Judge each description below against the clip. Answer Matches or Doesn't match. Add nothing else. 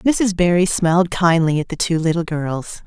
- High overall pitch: Doesn't match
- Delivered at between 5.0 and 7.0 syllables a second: Doesn't match